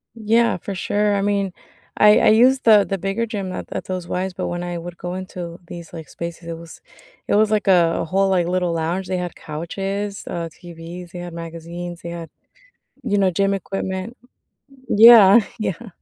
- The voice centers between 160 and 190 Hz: Yes, medium, 185 Hz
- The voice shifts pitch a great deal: No, average, 2.9 semitones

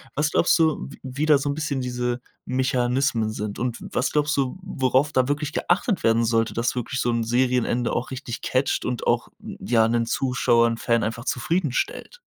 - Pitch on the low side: Yes, low, 125 Hz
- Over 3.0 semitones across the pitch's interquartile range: Yes, average, 3.5 semitones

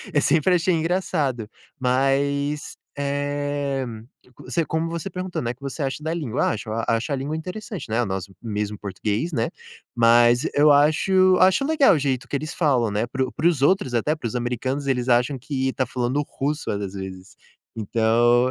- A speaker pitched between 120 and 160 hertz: Yes, low, 135 Hz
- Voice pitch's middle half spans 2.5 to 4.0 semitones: No, average, 4.4 semitones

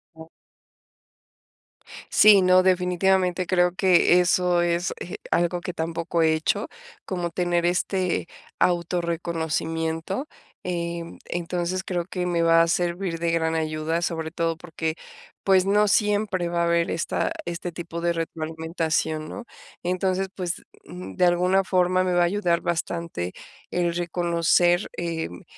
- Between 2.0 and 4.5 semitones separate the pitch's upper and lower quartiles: No, narrow, 1.5 semitones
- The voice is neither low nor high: Yes, medium, 175 Hz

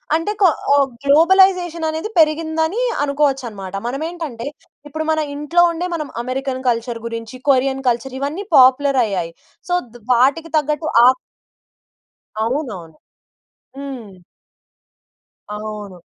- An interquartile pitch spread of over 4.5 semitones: Yes, average, 4.9 semitones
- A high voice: Yes, very high, 275 Hz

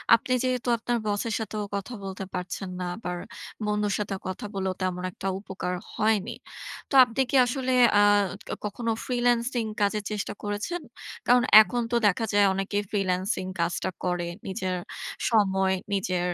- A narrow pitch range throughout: No, average, 3.5 semitones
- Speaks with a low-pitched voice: No, high, 205 Hz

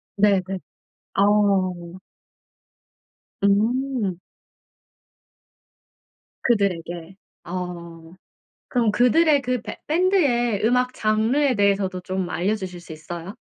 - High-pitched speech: Yes, high, 205 Hz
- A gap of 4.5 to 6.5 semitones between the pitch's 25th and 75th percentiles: Yes, wide, 5.4 semitones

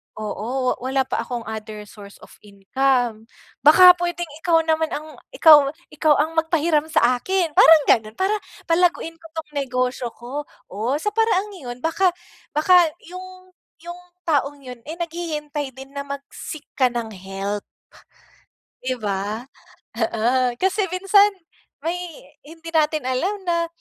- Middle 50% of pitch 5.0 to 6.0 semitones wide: Yes, wide, 5.5 semitones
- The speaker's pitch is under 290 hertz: No, very high, 295 Hz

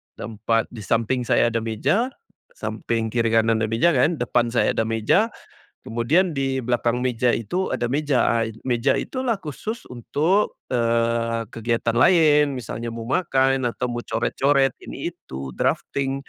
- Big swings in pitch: No, average, 3.3 semitones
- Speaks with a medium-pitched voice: No, low, 120 Hz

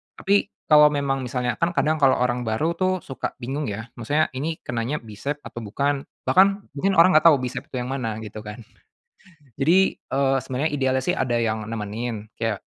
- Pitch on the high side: No, low, 130 Hz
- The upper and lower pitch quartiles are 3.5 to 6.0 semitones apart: Yes, average, 4.6 semitones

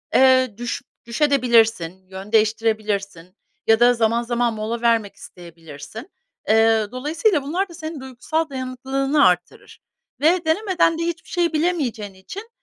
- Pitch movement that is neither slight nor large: No, wide, 6.0 semitones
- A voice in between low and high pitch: No, high, 240 Hz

